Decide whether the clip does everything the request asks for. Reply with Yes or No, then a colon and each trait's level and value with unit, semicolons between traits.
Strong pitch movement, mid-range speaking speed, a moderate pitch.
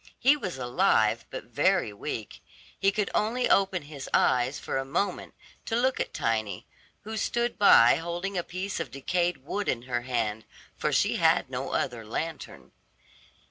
Yes: wide, 8.5 semitones; average, 165 wpm; medium, 165 Hz